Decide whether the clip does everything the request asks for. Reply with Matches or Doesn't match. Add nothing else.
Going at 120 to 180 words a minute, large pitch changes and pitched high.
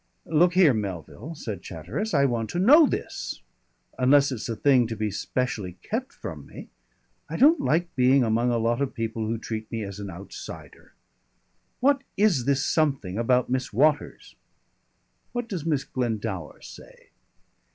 Doesn't match